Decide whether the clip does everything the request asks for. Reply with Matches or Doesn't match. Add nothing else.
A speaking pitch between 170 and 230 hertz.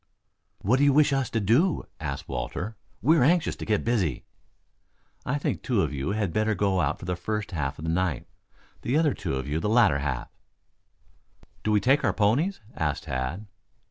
Doesn't match